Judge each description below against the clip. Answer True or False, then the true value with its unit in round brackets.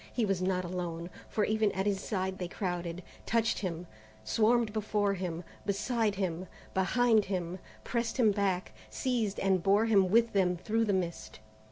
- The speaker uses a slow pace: False (165 wpm)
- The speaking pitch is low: False (195 Hz)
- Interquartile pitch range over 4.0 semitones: False (3.1 semitones)